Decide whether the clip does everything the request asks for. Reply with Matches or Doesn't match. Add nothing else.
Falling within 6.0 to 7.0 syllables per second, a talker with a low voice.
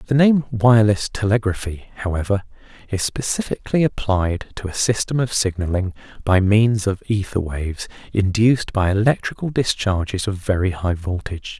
Doesn't match